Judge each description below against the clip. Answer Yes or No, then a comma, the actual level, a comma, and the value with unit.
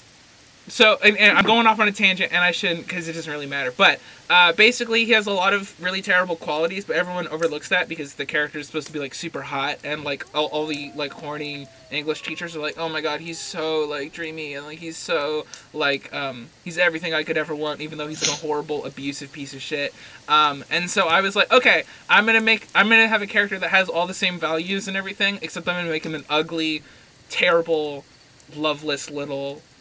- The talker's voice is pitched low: No, medium, 160 Hz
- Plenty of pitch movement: No, average, 3.9 semitones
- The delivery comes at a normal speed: No, fast, 230 wpm